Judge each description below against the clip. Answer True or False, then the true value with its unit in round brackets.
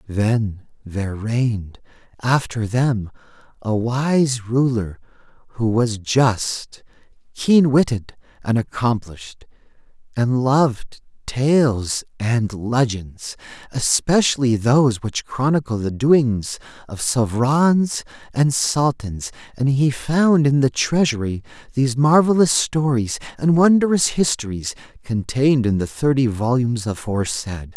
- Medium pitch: False (125 Hz)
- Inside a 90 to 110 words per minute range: True (105 wpm)